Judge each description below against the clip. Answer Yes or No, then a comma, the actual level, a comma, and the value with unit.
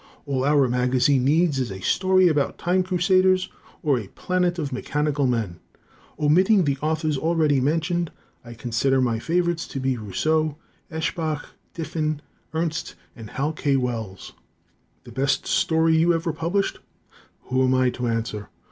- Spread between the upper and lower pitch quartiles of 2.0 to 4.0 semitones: No, average, 4.5 semitones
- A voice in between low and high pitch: Yes, medium, 150 Hz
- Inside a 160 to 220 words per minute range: No, average, 145 wpm